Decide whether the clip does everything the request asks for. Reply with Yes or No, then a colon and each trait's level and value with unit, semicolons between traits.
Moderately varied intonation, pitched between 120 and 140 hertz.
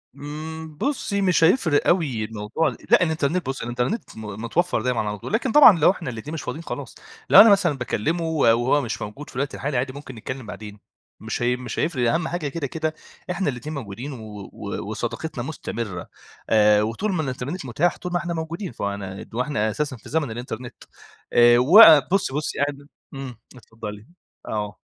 No: wide, 5.8 semitones; low, 135 Hz